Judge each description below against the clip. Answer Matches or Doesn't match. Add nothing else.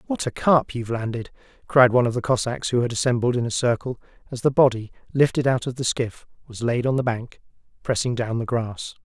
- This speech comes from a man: Matches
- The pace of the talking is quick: Matches